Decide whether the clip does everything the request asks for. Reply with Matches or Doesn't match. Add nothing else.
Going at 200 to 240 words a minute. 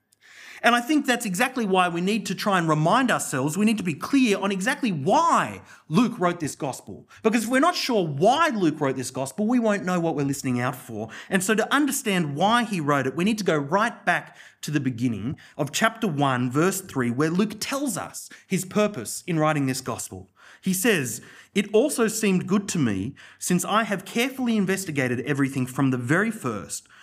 Matches